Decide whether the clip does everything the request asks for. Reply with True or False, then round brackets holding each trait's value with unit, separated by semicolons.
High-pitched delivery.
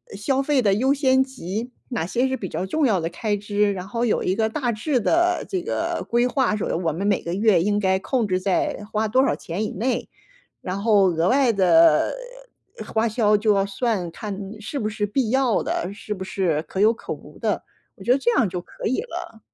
True (215 Hz)